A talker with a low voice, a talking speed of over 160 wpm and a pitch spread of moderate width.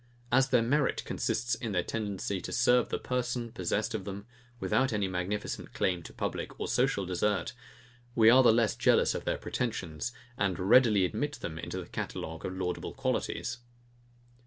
Yes: low, 110 Hz; average, 170 wpm; average, 4.6 semitones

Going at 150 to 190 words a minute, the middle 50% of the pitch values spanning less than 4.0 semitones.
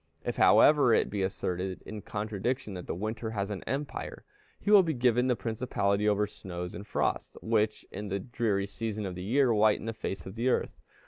No: average, 200 wpm; average, 3.3 semitones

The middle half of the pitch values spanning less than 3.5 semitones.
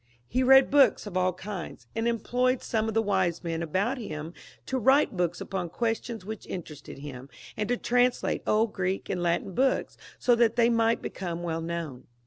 No: wide, 5.4 semitones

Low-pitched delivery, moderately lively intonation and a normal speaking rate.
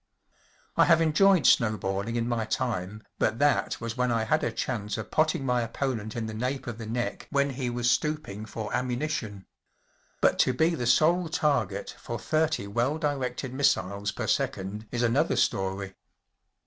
Yes: low, 120 Hz; average, 4.5 semitones; average, 170 wpm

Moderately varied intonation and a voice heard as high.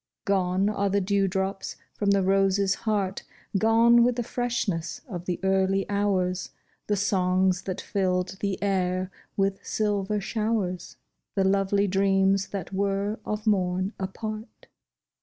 No: narrow, 1.5 semitones; high, 195 Hz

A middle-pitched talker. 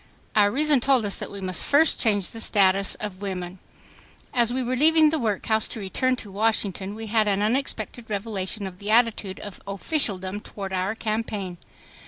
No: high, 210 Hz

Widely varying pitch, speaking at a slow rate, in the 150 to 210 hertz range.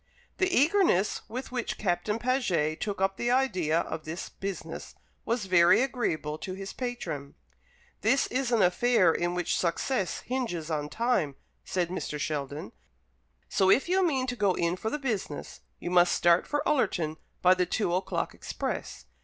No: wide, 6.4 semitones; average, 160 wpm; high, 190 Hz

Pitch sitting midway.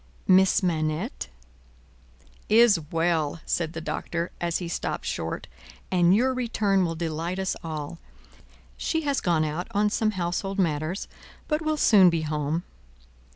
Yes: medium, 175 Hz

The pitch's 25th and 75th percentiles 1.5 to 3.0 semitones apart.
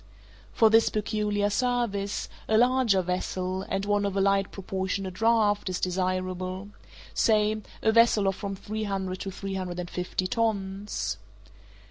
Yes: narrow, 2.4 semitones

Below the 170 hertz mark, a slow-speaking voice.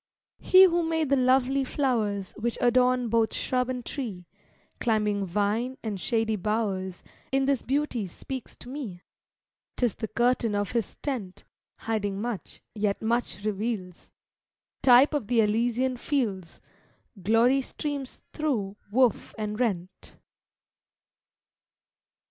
No: high, 230 Hz; slow, 120 wpm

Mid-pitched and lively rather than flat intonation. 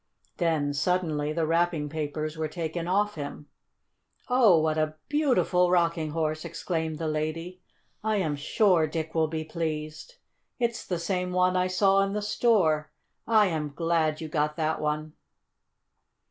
No: medium, 165 Hz; average, 2.9 semitones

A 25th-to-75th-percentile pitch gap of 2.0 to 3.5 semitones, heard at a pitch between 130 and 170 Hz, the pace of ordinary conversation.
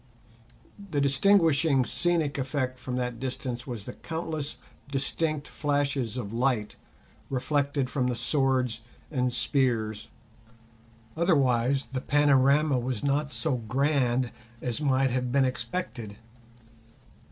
No: narrow, 2.6 semitones; low, 135 Hz; slow, 110 wpm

